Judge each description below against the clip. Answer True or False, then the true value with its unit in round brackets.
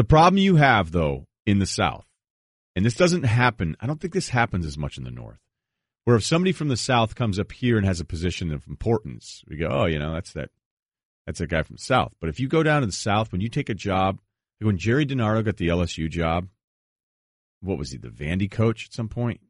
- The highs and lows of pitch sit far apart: True (6.2 semitones)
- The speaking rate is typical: False (245 wpm)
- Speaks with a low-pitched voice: True (105 Hz)